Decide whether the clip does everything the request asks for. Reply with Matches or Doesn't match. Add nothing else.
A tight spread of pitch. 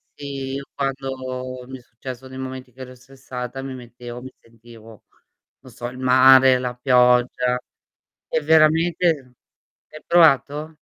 Matches